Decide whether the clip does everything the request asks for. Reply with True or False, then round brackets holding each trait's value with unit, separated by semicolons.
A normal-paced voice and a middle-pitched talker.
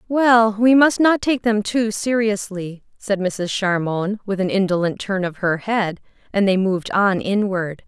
False (175 wpm; 205 Hz)